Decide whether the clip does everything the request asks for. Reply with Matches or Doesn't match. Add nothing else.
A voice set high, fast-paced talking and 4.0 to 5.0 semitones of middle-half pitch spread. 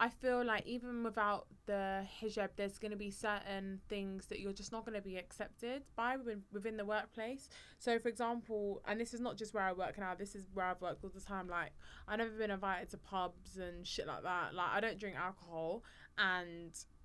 Doesn't match